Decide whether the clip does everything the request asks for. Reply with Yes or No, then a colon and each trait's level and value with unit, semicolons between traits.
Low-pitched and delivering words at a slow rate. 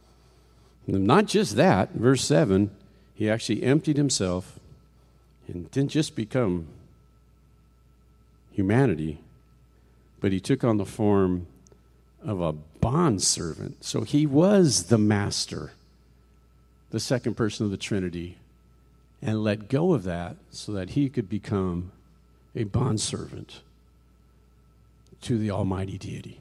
Yes: very low, 95 Hz; slow, 120 wpm